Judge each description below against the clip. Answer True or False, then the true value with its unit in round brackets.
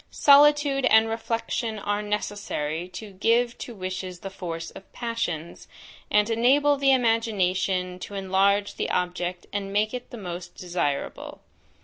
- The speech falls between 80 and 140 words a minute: True (135 wpm)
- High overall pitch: True (205 Hz)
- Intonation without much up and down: False (4.1 semitones)